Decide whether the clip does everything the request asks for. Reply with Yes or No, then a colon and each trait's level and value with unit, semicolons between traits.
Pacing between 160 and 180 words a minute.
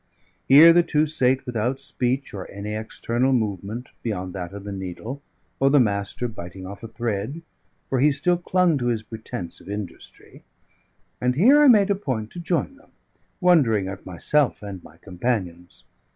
Yes: average, 170 wpm